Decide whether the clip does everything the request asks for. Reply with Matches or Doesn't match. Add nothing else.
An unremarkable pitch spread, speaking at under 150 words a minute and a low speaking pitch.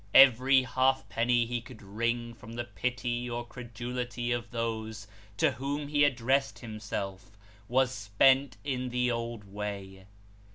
Doesn't match